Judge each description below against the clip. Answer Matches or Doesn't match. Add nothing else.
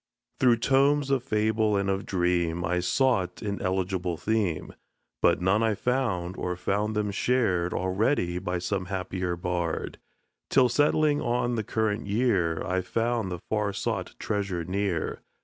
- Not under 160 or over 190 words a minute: Doesn't match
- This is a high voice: Doesn't match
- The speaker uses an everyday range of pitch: Matches